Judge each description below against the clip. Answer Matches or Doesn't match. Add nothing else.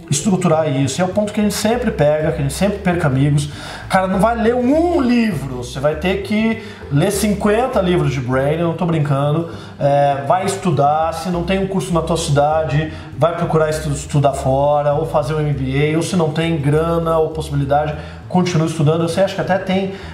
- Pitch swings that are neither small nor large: Matches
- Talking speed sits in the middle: Doesn't match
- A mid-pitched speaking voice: Matches